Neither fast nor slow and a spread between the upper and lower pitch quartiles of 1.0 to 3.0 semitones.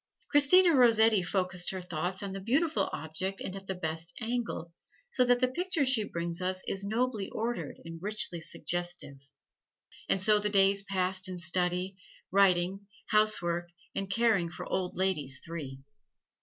No: average, 150 wpm; average, 3.6 semitones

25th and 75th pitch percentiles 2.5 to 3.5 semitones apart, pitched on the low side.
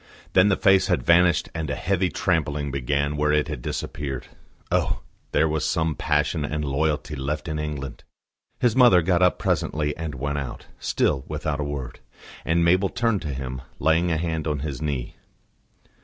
Yes: average, 2.8 semitones; very low, 75 Hz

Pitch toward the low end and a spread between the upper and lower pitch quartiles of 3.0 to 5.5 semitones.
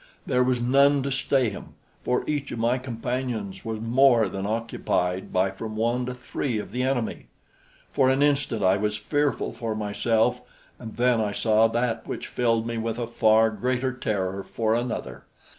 No: low, 115 Hz; narrow, 2.6 semitones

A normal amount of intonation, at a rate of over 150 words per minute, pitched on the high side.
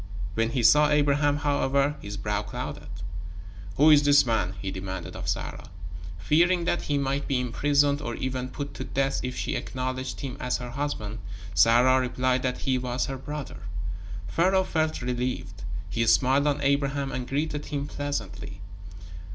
No: average, 3.0 semitones; average, 160 wpm; low, 135 Hz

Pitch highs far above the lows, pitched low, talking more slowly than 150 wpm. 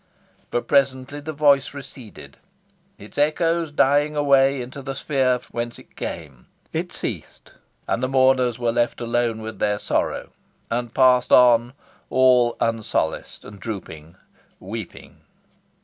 No: average, 3.1 semitones; low, 125 Hz; slow, 135 wpm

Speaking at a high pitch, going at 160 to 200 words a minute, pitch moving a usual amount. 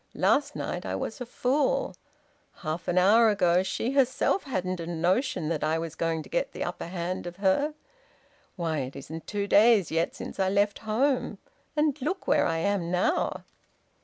No: high, 195 Hz; average, 180 wpm; wide, 7.4 semitones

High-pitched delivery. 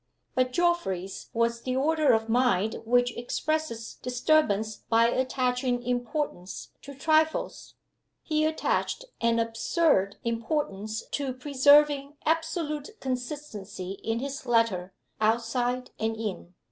Yes: high, 245 Hz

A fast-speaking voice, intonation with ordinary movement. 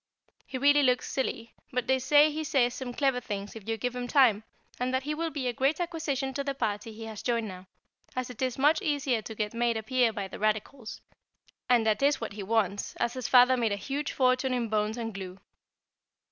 Yes: fast, 230 wpm; average, 3.6 semitones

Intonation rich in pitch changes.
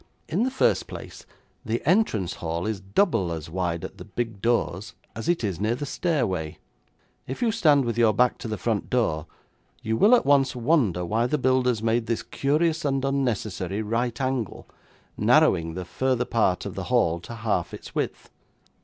Yes: wide, 5.7 semitones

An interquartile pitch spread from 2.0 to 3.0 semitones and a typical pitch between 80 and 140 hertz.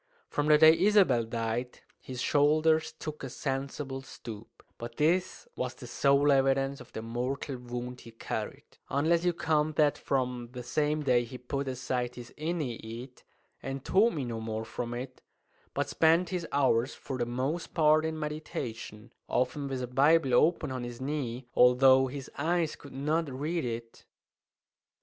No: average, 3.8 semitones; low, 135 Hz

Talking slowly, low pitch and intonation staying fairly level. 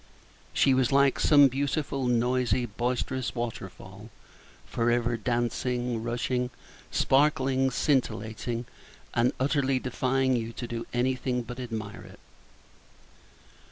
Yes: slow, 110 wpm; low, 125 Hz; narrow, 1.9 semitones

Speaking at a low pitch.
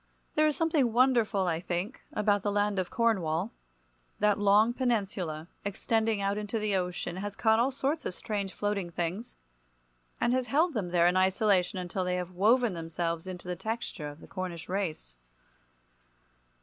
No: high, 200 Hz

